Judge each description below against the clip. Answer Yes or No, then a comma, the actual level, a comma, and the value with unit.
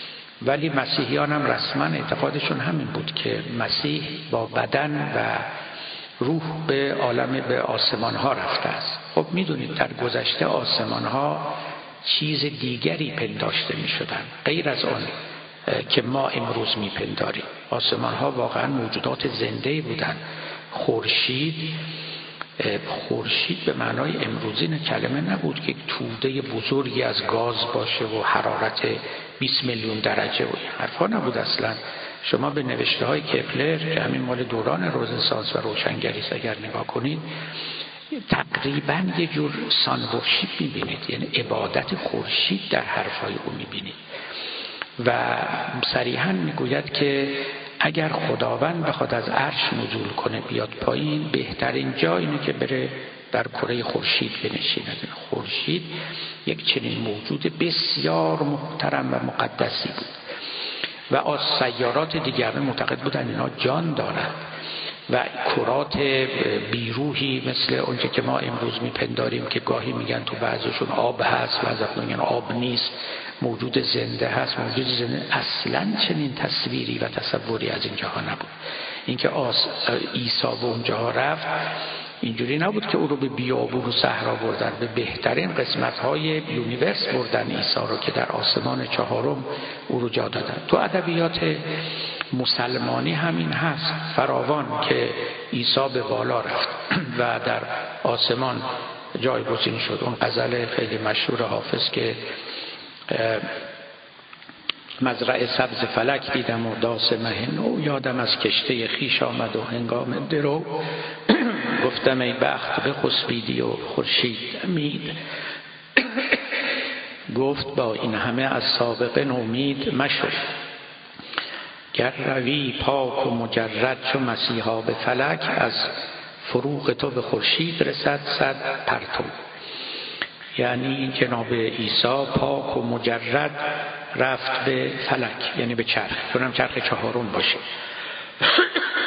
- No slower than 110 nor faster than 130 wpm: Yes, average, 125 wpm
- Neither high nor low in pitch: No, low, 130 Hz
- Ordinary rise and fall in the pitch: Yes, average, 4.0 semitones